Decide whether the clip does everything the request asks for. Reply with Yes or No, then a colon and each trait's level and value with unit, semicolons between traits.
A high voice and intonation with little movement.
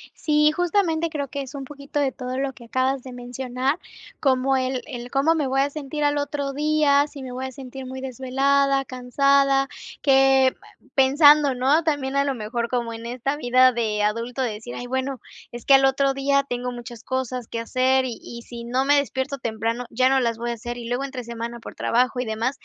Yes: very high, 260 Hz; narrow, 2.3 semitones